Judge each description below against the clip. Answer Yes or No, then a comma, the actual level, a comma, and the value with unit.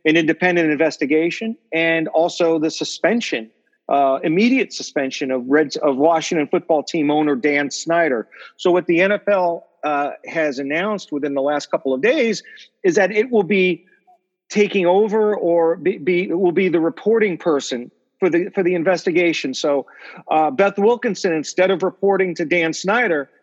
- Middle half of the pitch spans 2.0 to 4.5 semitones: Yes, average, 4.1 semitones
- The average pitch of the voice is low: No, medium, 170 Hz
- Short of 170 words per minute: Yes, average, 155 wpm